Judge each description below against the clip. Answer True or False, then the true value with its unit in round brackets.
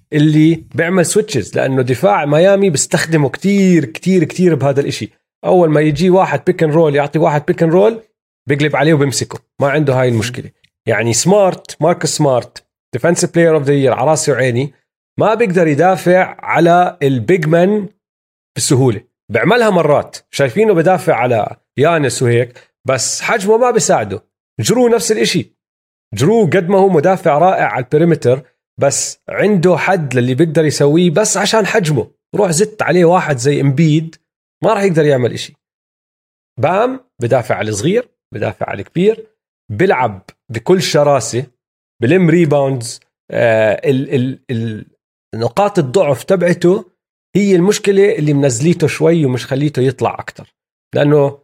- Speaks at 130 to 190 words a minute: True (135 wpm)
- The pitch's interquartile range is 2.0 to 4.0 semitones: False (5.0 semitones)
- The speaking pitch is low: False (160 Hz)